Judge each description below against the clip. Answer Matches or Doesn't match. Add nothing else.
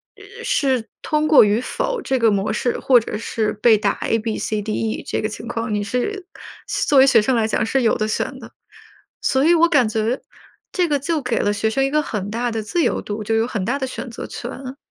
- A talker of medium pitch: Doesn't match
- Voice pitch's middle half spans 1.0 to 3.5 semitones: Doesn't match